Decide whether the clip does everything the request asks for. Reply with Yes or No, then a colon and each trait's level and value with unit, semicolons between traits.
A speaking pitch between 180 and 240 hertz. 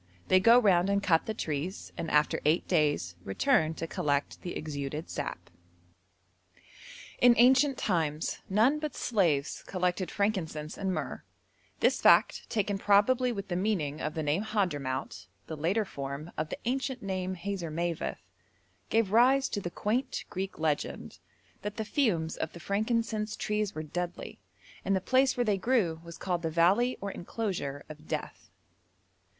Yes: medium, 185 Hz